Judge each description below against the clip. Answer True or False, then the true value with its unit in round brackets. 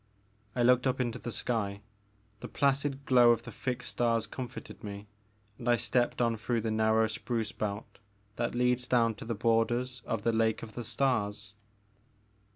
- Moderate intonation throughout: False (2.0 semitones)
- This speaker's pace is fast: False (170 wpm)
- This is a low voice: True (115 Hz)